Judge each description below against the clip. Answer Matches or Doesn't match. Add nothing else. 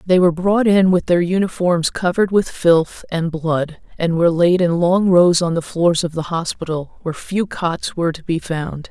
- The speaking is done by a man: Doesn't match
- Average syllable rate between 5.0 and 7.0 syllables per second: Doesn't match